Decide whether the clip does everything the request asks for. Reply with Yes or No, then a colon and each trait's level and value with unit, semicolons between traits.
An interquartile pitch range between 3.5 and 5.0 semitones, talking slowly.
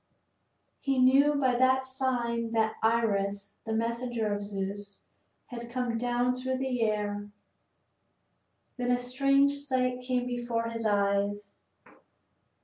No: average, 3.1 semitones; slow, 120 wpm